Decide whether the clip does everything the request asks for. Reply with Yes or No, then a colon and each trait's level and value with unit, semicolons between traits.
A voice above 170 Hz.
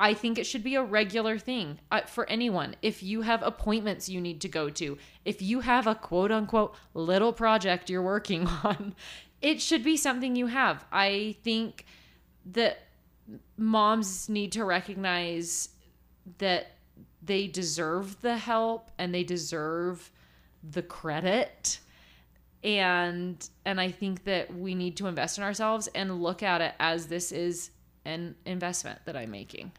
Yes: high, 190 Hz